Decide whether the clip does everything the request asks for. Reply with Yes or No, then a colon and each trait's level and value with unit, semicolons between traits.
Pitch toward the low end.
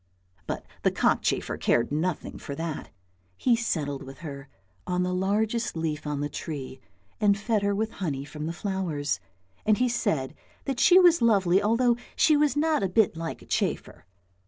No: medium, 185 Hz